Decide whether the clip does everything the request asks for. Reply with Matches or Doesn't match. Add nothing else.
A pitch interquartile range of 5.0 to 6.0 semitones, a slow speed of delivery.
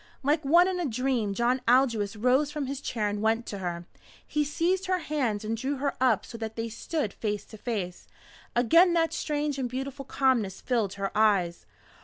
Doesn't match